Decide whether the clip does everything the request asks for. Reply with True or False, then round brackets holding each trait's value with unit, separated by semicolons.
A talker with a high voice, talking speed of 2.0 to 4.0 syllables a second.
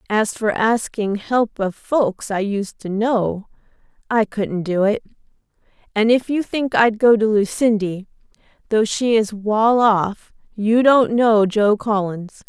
True (215 Hz; 3.7 syllables/s)